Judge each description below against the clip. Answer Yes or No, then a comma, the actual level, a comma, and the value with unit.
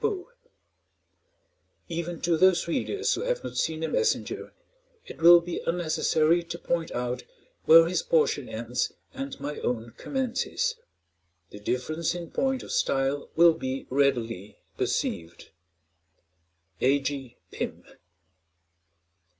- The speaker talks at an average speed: No, slow, 120 wpm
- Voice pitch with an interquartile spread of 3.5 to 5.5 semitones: Yes, average, 4.7 semitones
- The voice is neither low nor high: Yes, medium, 165 Hz